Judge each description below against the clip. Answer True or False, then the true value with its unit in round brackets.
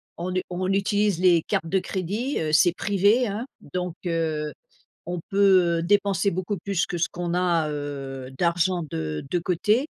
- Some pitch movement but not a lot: True (3.1 semitones)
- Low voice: False (180 Hz)